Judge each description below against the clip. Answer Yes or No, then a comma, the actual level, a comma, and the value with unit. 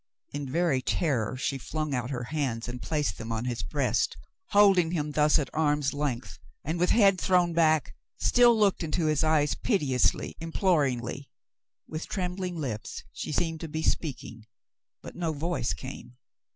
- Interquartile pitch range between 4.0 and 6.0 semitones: Yes, average, 4.9 semitones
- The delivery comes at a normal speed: Yes, average, 165 wpm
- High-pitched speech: No, medium, 150 Hz